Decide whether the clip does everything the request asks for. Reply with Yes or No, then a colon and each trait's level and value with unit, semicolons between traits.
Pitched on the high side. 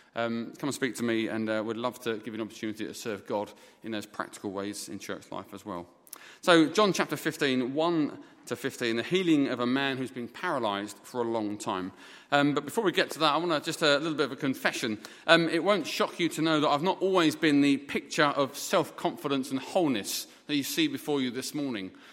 No: low, 135 Hz